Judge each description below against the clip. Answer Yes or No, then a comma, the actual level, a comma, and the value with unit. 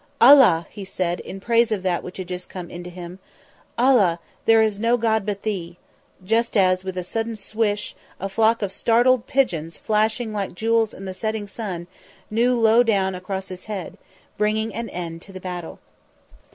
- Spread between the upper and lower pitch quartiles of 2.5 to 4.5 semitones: Yes, average, 3.5 semitones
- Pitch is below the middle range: No, high, 205 Hz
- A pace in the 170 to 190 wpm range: Yes, average, 180 wpm